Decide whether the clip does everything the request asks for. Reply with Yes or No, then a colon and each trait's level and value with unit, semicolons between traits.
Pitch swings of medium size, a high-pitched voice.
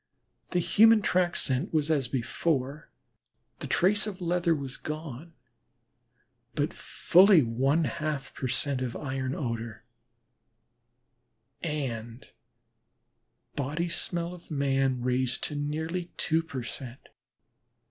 No: average, 4.5 semitones; medium, 145 Hz